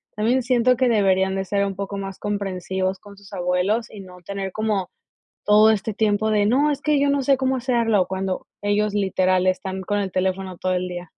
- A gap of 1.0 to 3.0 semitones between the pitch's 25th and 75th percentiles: Yes, average, 2.7 semitones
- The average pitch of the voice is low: No, high, 200 Hz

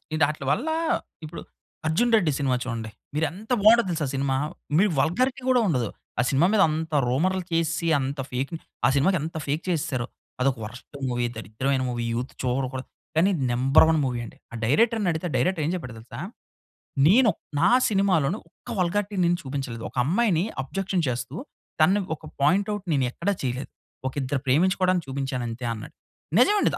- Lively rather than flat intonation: Yes, wide, 6.3 semitones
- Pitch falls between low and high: Yes, medium, 155 Hz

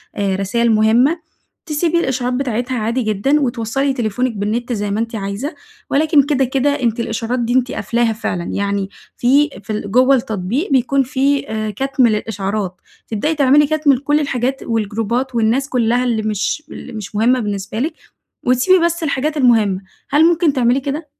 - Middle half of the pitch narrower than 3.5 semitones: No, average, 4.2 semitones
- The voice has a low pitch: No, high, 245 Hz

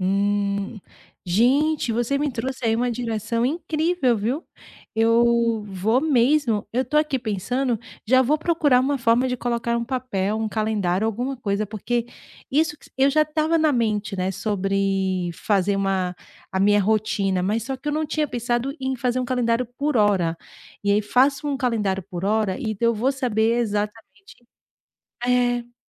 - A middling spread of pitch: Yes, average, 4.1 semitones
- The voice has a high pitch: Yes, high, 230 Hz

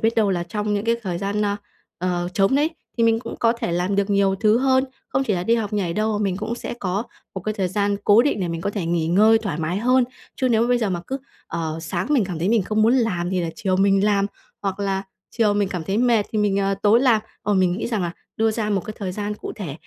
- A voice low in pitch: No, high, 205 Hz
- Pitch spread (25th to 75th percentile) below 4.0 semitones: Yes, average, 3.2 semitones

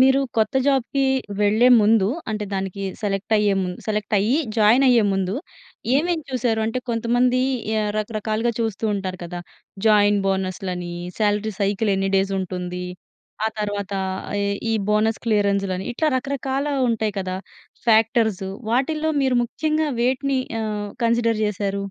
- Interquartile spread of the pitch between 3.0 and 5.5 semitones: Yes, average, 3.4 semitones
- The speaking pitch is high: Yes, high, 215 Hz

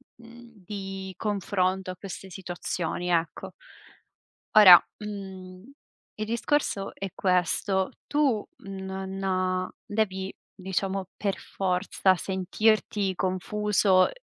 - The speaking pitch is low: No, high, 190 Hz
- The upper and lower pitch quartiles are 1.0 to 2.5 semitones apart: Yes, narrow, 2.0 semitones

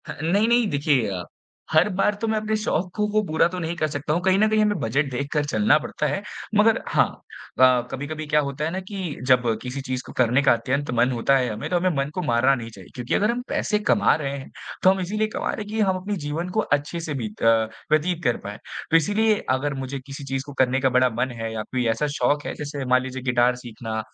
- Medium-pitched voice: Yes, medium, 145 Hz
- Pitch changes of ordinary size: No, wide, 6.3 semitones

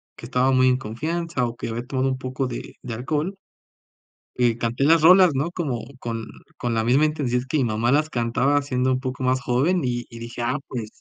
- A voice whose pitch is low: Yes, low, 130 Hz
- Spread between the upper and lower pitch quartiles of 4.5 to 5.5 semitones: No, average, 3.3 semitones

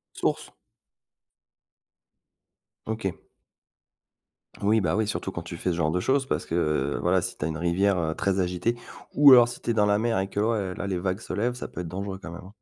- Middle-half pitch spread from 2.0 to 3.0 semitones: No, average, 3.9 semitones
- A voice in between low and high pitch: No, very low, 95 Hz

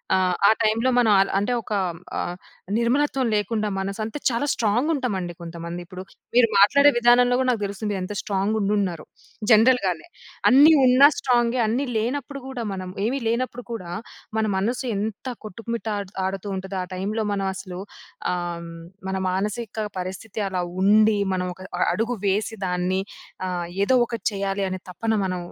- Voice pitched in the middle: No, high, 210 Hz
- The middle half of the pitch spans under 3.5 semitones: No, average, 4.1 semitones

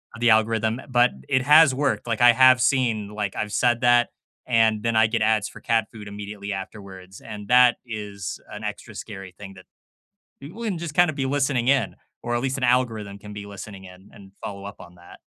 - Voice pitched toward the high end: No, low, 110 Hz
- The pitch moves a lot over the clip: No, average, 3.6 semitones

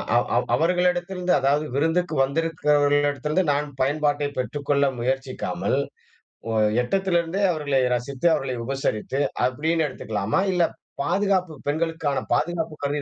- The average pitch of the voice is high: No, medium, 150 Hz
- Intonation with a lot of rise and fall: No, average, 3.5 semitones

